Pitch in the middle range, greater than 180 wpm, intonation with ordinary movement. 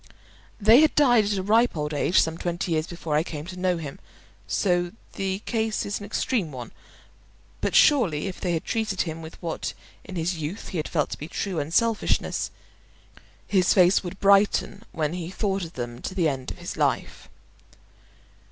Yes: medium, 180 Hz; average, 190 wpm; average, 4.0 semitones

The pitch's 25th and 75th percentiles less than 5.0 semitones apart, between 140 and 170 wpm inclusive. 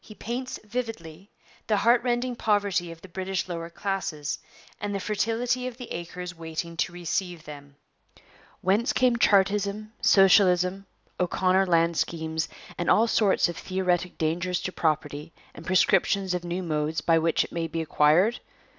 Yes: average, 3.6 semitones; average, 155 wpm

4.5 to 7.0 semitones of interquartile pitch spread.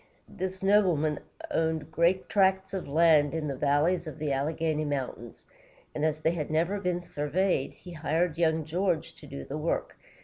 No: average, 3.2 semitones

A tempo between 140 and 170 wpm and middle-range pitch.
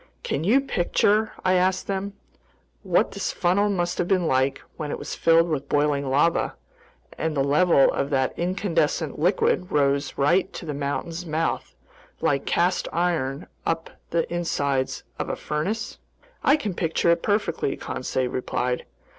Yes: average, 155 wpm; medium, 165 Hz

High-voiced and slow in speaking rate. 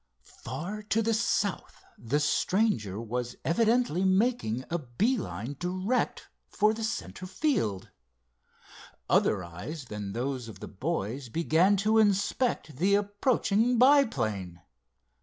No: medium, 175 Hz; slow, 120 wpm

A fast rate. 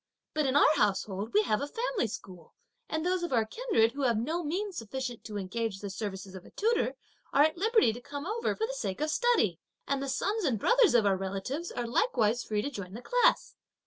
Yes: fast, 225 wpm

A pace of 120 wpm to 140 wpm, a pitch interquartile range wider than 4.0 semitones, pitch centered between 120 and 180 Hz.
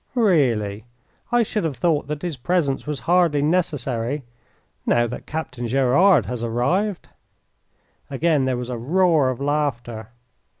Yes: slow, 135 wpm; wide, 5.6 semitones; medium, 140 Hz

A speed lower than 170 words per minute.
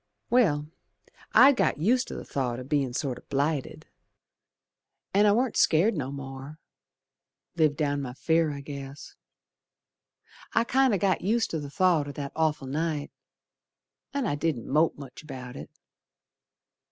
Yes: average, 150 wpm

